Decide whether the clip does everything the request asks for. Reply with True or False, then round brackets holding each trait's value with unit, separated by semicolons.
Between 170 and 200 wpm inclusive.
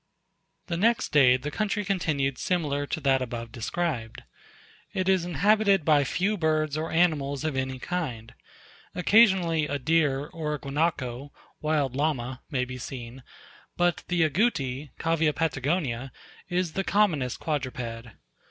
False (135 wpm)